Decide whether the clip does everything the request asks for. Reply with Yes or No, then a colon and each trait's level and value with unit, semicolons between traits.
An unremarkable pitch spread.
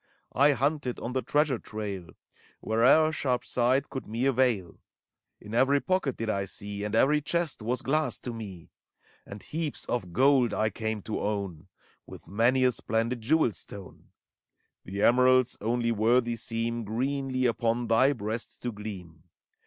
Yes: average, 3.6 semitones